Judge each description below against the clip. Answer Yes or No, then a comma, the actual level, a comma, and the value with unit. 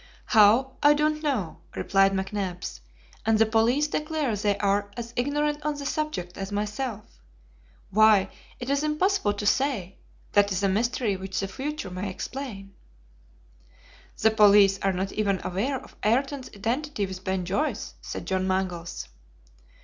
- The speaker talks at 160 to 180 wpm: No, average, 150 wpm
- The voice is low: No, high, 210 Hz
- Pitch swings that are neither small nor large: No, wide, 5.9 semitones